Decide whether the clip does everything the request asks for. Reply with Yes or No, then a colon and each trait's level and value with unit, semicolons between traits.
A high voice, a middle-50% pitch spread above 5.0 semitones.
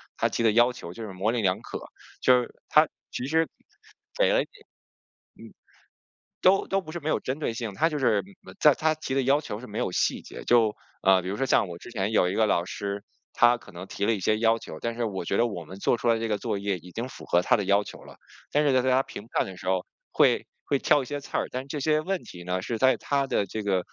No: low, 115 Hz; wide, 5.4 semitones